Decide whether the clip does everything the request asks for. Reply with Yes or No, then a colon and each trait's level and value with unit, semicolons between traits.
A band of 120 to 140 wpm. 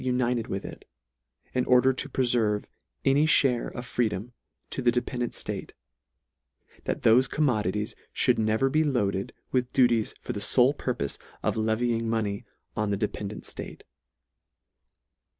Yes: slow, 135 wpm